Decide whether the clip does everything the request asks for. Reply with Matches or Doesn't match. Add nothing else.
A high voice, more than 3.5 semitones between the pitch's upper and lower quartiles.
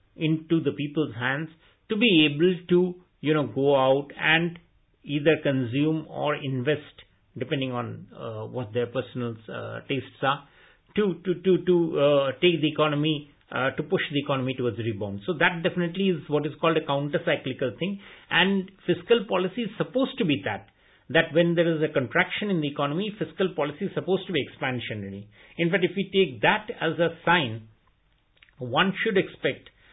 Doesn't match